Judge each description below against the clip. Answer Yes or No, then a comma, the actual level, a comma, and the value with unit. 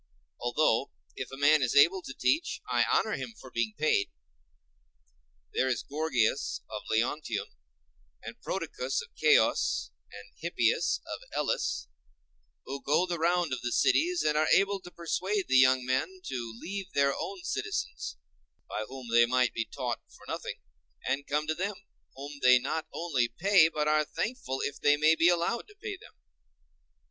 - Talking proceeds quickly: No, average, 165 wpm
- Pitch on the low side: No, medium, 145 Hz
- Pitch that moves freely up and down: Yes, wide, 5.8 semitones